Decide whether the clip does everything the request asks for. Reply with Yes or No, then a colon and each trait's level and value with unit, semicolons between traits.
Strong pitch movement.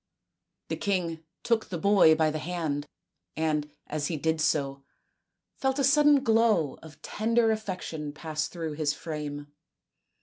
Yes: wide, 6.0 semitones